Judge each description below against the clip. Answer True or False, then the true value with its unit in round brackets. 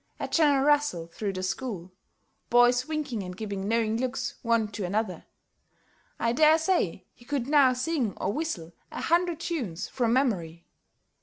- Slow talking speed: False (155 wpm)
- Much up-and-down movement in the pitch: True (6.5 semitones)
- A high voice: True (240 Hz)